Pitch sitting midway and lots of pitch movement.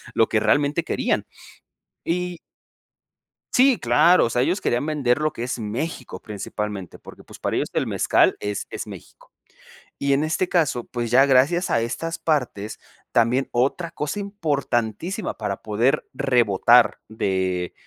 No: low, 125 Hz; wide, 6.2 semitones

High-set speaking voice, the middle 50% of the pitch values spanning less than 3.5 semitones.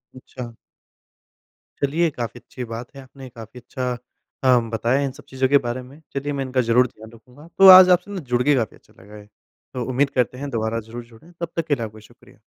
No: low, 125 Hz; average, 3.1 semitones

